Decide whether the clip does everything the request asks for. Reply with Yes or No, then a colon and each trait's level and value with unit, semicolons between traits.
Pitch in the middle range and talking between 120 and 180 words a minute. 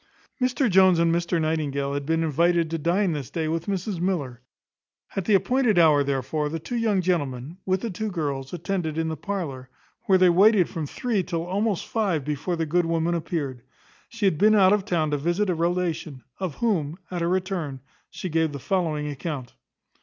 No: medium, 170 Hz; average, 195 wpm